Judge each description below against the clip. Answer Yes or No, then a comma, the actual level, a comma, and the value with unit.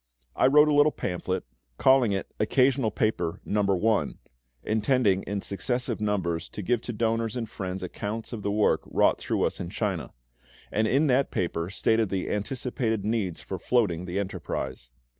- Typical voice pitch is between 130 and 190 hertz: No, low, 105 Hz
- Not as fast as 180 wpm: Yes, average, 165 wpm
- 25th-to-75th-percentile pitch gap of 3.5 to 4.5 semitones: Yes, average, 4.1 semitones